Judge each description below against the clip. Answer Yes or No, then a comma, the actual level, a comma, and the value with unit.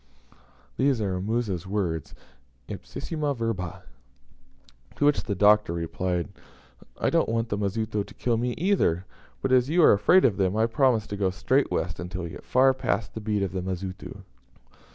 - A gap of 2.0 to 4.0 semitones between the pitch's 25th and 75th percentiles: No, average, 4.8 semitones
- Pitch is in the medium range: No, low, 105 Hz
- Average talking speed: Yes, average, 175 wpm